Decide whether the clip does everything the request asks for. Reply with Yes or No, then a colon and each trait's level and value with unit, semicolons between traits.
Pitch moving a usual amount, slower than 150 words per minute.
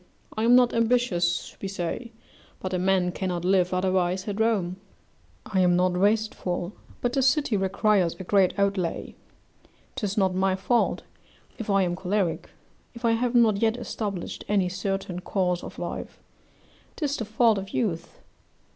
No: average, 3.4 semitones; average, 155 wpm